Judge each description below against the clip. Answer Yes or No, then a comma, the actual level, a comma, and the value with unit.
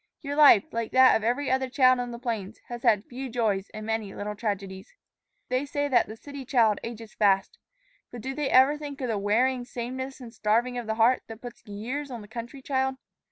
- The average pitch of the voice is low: No, high, 240 Hz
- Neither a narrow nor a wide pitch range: Yes, average, 3.2 semitones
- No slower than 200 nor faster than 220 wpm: Yes, fast, 205 wpm